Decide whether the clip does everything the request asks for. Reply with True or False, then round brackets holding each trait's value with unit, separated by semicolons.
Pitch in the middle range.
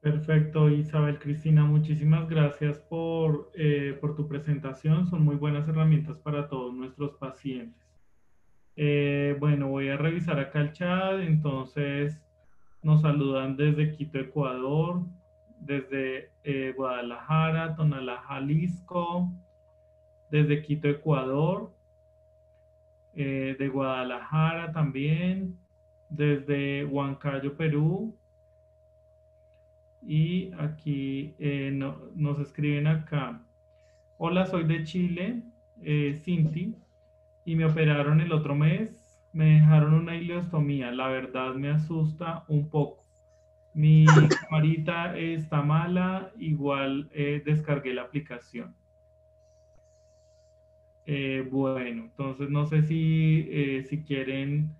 True (145 Hz)